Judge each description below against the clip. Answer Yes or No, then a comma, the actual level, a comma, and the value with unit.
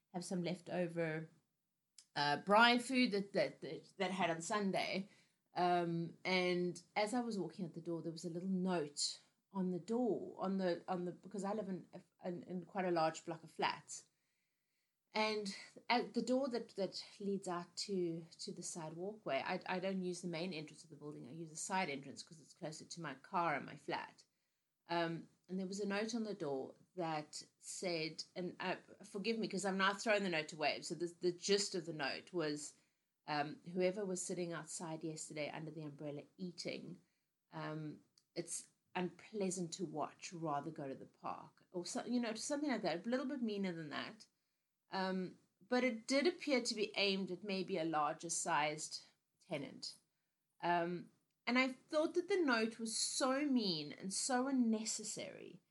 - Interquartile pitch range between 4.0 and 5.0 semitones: No, average, 3.6 semitones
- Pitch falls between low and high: Yes, medium, 180 Hz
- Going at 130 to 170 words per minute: No, average, 185 wpm